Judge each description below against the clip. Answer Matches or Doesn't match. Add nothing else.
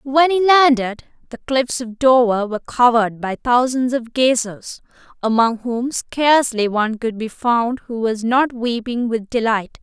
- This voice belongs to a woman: Matches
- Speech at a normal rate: Matches